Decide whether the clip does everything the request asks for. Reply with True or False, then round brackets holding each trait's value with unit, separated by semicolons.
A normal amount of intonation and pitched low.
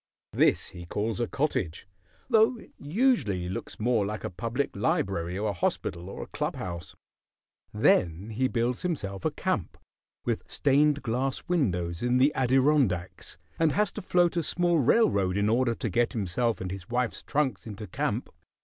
False (6.9 semitones; 115 Hz)